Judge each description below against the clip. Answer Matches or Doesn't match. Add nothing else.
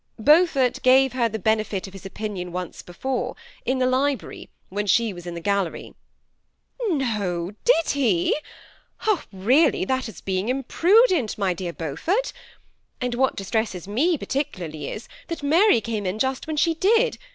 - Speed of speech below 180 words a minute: Matches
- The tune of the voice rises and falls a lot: Matches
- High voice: Matches